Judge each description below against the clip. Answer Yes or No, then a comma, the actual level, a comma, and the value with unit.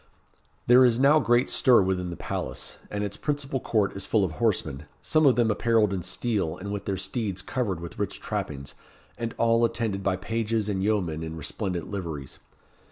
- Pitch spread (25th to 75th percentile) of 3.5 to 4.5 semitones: Yes, average, 4.2 semitones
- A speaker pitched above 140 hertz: No, low, 105 Hz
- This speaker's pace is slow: No, average, 185 wpm